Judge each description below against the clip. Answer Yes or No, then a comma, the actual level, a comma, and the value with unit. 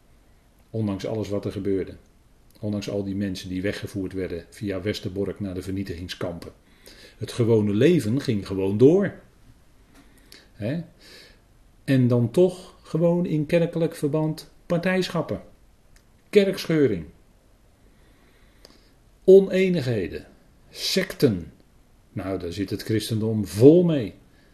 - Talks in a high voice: No, low, 105 Hz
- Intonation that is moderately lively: No, wide, 7.7 semitones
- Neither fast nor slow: No, slow, 100 wpm